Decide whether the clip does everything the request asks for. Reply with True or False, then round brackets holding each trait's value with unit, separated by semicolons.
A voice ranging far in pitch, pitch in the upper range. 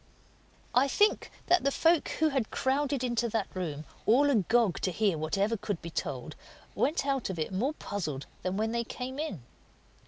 True (6.6 semitones; 230 Hz)